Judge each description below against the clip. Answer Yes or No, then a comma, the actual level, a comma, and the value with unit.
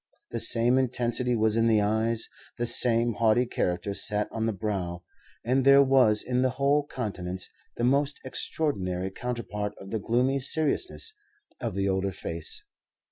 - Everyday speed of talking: Yes, average, 155 wpm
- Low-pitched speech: Yes, low, 115 Hz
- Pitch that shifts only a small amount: No, average, 3.8 semitones